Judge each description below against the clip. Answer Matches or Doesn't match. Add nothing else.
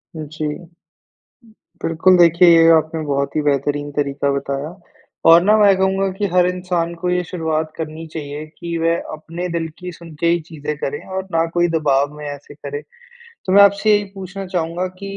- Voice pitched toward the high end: Doesn't match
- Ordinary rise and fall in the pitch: Matches